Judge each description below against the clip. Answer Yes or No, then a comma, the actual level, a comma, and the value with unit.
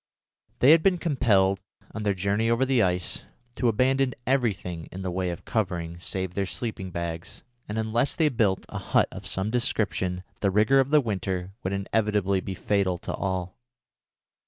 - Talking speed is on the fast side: No, average, 175 wpm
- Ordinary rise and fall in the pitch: Yes, average, 4.2 semitones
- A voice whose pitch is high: No, low, 100 Hz